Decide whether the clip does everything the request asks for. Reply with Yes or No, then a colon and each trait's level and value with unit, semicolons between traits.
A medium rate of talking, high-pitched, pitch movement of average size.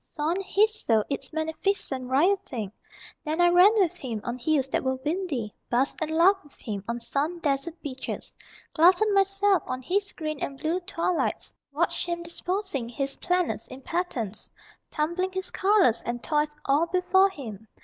No: average, 165 wpm; very high, 315 Hz; wide, 6.0 semitones